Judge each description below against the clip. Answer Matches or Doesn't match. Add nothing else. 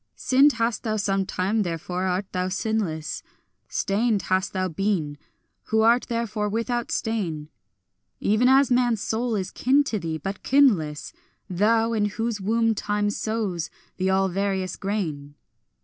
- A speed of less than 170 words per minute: Matches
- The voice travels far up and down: Doesn't match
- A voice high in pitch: Matches